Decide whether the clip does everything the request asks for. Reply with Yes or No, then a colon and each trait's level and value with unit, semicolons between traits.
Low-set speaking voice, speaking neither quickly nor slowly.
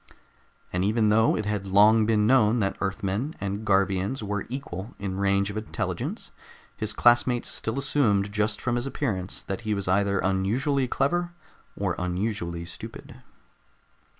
Yes: low, 105 Hz; average, 150 wpm